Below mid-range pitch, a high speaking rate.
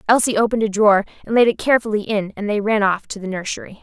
No: high, 210 Hz; fast, 250 wpm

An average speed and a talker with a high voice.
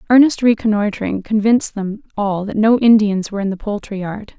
Yes: average, 180 wpm; high, 210 Hz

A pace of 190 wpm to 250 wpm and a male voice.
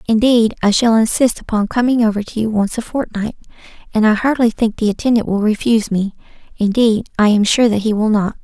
No: average, 200 wpm; female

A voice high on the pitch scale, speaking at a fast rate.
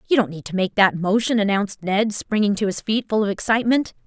Yes: high, 205 Hz; fast, 235 wpm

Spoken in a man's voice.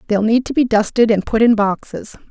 No: female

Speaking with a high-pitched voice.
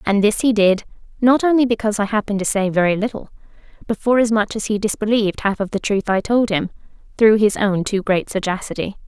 Yes: high, 210 Hz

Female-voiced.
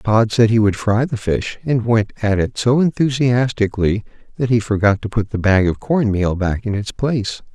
No: male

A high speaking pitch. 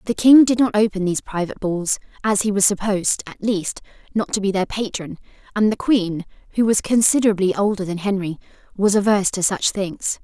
Yes: high, 200 Hz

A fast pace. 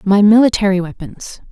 No: slow, 120 wpm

